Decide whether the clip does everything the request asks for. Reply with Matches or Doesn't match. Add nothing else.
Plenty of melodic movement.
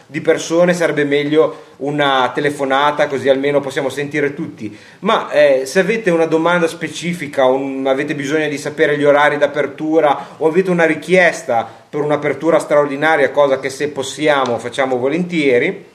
Doesn't match